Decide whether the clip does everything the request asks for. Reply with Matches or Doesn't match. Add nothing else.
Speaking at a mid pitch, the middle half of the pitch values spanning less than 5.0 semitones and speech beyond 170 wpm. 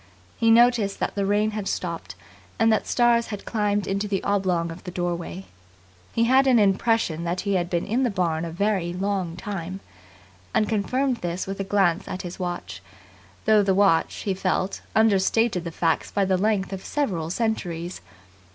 Doesn't match